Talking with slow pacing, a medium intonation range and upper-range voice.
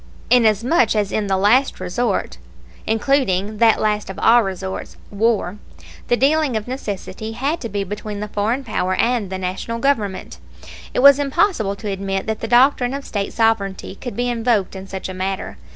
No: average, 175 wpm; average, 3.8 semitones; high, 215 Hz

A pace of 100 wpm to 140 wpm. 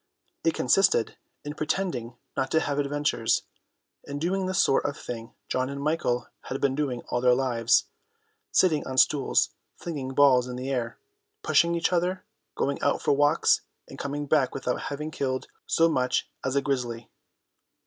No: average, 165 wpm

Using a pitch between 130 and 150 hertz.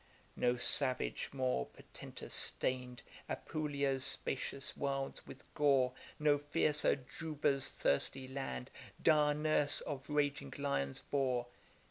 Yes: medium, 140 Hz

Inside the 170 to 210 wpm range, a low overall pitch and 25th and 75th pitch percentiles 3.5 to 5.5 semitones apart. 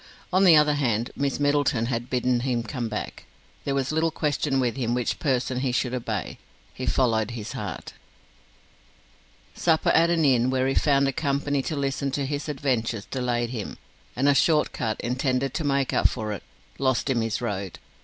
No: average, 185 wpm; low, 130 Hz; average, 3.1 semitones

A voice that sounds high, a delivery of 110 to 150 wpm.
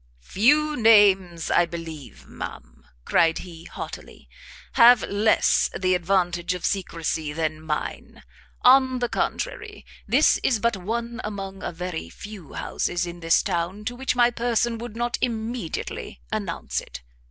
Yes: high, 195 Hz; average, 140 wpm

